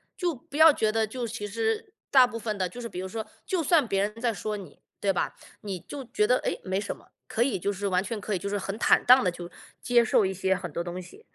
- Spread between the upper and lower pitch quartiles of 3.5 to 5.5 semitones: Yes, average, 4.3 semitones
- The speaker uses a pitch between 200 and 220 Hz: Yes, high, 210 Hz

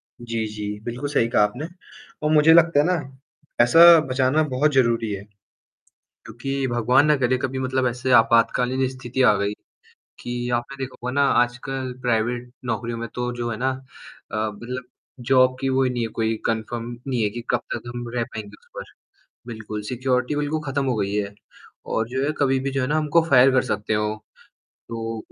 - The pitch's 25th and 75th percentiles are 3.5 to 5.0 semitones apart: No, narrow, 2.6 semitones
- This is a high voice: No, low, 125 Hz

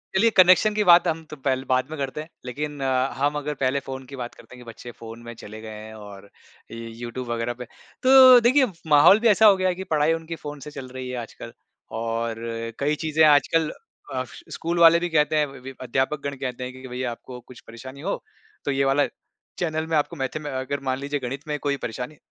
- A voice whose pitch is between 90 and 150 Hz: Yes, medium, 140 Hz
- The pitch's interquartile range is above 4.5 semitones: No, average, 3.8 semitones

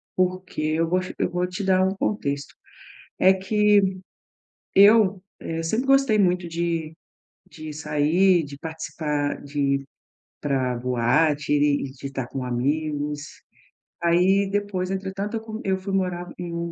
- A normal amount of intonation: Yes, average, 4.5 semitones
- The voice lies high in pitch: No, medium, 170 Hz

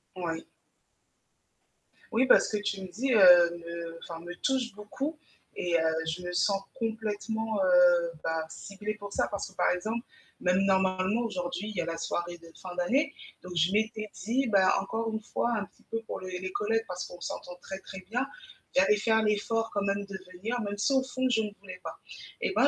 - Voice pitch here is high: Yes, high, 200 Hz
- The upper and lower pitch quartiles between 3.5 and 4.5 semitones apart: Yes, average, 3.8 semitones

